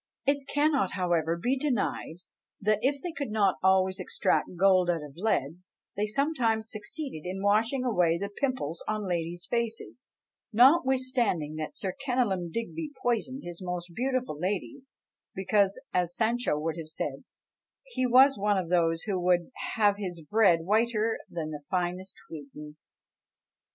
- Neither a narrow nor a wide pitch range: No, wide, 6.0 semitones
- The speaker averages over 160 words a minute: No, average, 145 wpm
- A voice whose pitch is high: Yes, high, 200 Hz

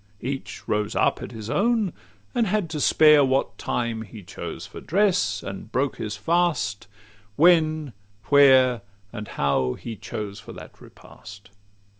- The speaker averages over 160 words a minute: No, average, 145 wpm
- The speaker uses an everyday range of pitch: No, wide, 7.0 semitones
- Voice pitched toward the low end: Yes, low, 130 Hz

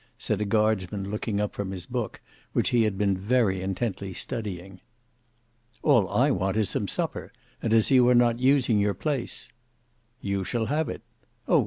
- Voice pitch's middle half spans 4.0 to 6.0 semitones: No, average, 3.6 semitones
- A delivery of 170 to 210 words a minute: Yes, average, 175 wpm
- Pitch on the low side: Yes, low, 105 Hz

